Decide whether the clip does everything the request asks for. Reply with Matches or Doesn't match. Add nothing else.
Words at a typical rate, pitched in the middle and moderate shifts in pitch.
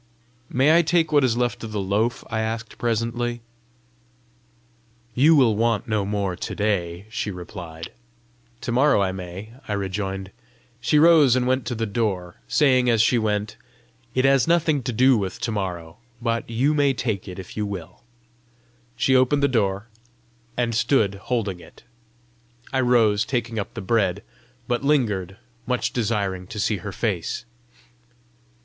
Doesn't match